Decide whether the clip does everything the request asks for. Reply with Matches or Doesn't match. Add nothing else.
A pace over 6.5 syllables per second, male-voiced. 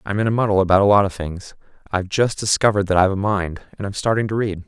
Matches